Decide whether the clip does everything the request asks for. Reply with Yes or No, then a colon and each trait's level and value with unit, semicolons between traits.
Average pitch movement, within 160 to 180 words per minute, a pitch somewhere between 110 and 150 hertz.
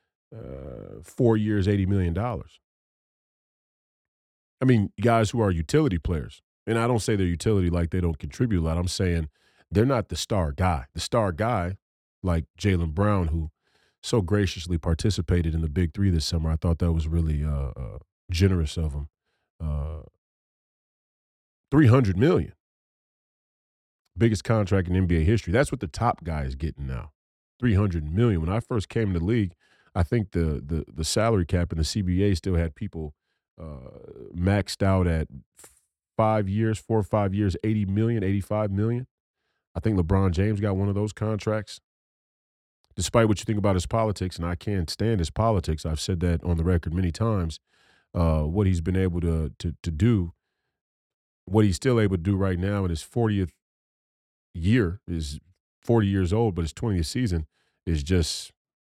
No: average, 4.6 semitones; average, 175 wpm; very low, 90 Hz